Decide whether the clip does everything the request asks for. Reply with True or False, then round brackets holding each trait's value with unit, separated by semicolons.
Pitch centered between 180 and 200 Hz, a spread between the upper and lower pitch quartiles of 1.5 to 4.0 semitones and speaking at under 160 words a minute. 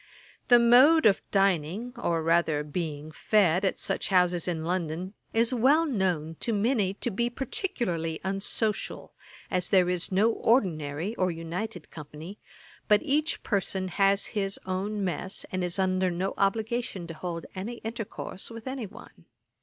False (190 Hz; 4.4 semitones; 150 wpm)